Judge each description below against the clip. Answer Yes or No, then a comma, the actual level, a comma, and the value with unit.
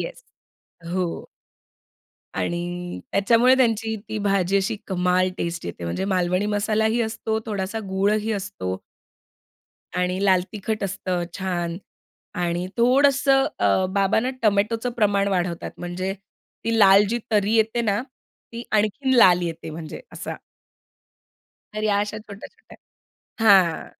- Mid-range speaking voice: No, high, 200 Hz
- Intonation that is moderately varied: Yes, average, 3.4 semitones